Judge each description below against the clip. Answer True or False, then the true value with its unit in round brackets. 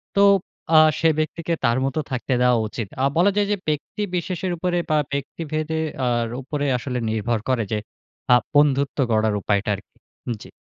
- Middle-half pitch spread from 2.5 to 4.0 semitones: False (5.6 semitones)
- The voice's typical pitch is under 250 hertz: True (140 Hz)